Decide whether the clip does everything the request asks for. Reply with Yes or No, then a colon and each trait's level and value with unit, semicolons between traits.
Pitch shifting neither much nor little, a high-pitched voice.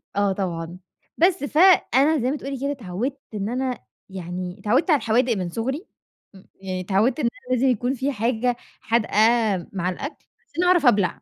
No: wide, 6.1 semitones; high, 240 Hz